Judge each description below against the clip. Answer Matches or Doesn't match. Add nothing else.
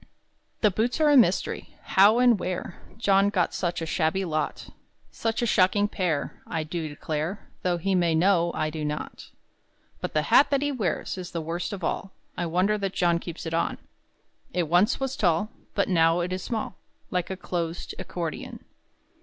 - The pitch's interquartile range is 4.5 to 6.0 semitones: Doesn't match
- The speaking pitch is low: Doesn't match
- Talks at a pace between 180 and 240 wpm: Matches